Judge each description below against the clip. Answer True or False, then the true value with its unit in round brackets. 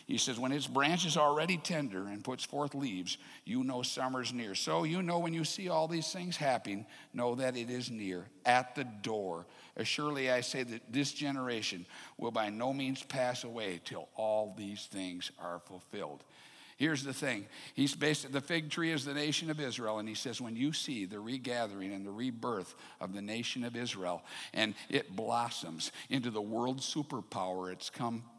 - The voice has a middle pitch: False (125 Hz)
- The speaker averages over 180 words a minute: True (190 wpm)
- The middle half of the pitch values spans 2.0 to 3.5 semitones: False (4.7 semitones)